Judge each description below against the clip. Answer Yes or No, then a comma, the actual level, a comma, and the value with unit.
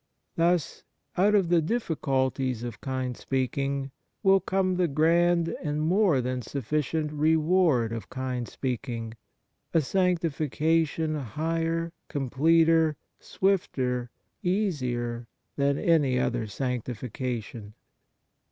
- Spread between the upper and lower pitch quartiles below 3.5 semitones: No, average, 4.8 semitones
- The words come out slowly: Yes, slow, 95 wpm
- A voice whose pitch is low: No, medium, 145 Hz